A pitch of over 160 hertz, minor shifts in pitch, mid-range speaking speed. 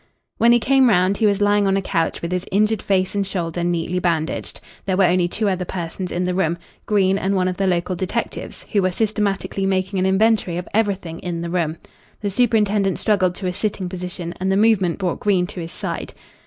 No: high, 190 Hz; narrow, 2.3 semitones; fast, 220 wpm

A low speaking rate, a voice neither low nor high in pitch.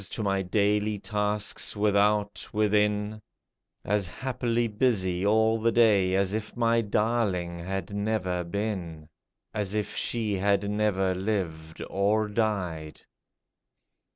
No: slow, 120 wpm; low, 105 Hz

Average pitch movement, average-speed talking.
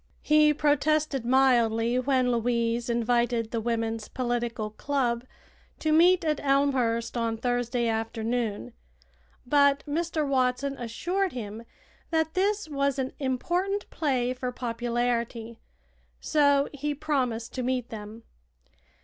No: average, 3.5 semitones; slow, 115 wpm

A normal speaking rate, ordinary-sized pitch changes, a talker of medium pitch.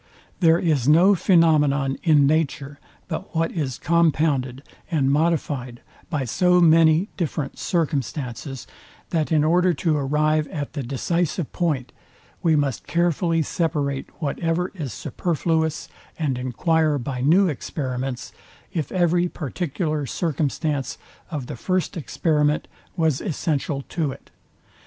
No: slow, 120 wpm; average, 3.3 semitones; medium, 155 Hz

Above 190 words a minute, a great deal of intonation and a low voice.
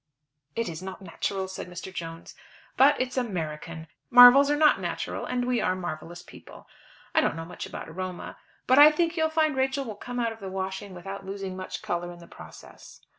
No: average, 200 wpm; wide, 6.4 semitones; high, 195 Hz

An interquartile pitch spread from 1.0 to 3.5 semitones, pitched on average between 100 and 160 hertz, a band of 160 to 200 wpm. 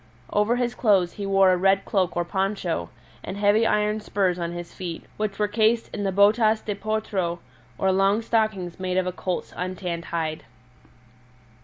No: average, 2.7 semitones; high, 195 Hz; average, 175 wpm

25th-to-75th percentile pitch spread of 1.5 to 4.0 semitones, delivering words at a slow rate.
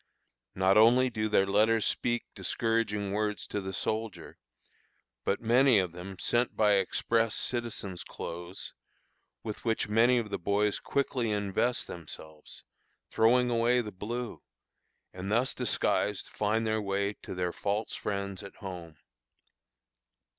Yes: average, 2.8 semitones; slow, 130 wpm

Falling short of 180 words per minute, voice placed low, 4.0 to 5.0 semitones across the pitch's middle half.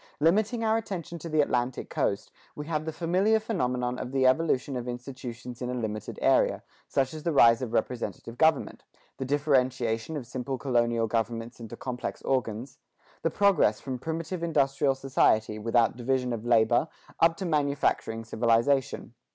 Yes: average, 160 wpm; low, 130 Hz; average, 4.7 semitones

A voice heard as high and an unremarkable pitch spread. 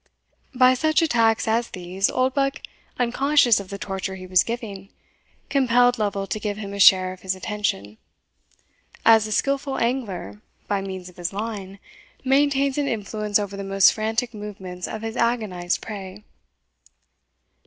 Yes: high, 210 Hz; average, 4.2 semitones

